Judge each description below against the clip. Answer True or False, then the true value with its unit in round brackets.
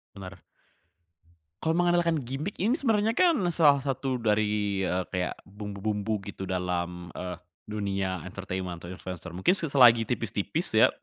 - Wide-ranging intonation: True (7.5 semitones)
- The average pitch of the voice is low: True (105 Hz)